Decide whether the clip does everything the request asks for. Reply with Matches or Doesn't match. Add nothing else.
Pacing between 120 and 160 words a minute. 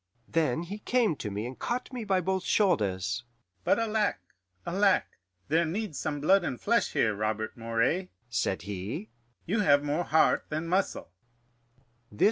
Matches